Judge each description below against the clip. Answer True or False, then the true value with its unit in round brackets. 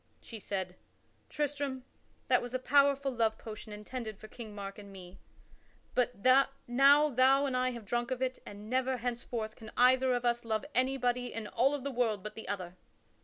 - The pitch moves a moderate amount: True (3.2 semitones)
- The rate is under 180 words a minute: False (185 wpm)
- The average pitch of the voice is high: True (245 Hz)